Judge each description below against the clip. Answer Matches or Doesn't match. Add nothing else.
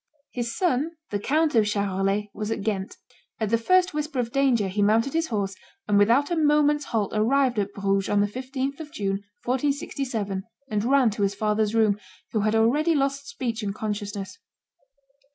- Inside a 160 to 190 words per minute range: Matches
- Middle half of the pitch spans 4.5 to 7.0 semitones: Matches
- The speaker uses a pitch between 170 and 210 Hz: Doesn't match